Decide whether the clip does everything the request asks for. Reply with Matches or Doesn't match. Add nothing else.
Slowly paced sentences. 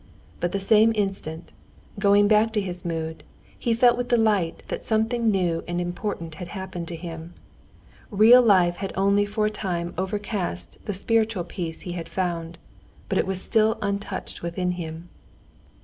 Doesn't match